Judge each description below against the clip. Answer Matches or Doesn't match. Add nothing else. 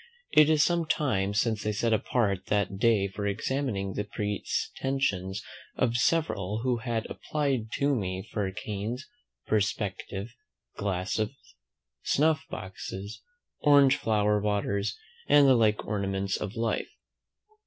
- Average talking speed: Doesn't match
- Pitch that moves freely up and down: Doesn't match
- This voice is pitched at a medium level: Doesn't match